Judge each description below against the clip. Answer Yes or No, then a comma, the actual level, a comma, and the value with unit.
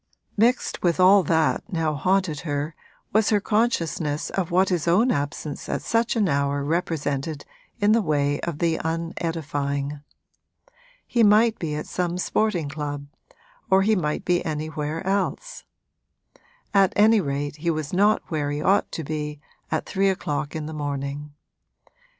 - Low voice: No, medium, 160 Hz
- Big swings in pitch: No, average, 4.7 semitones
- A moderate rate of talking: Yes, average, 150 wpm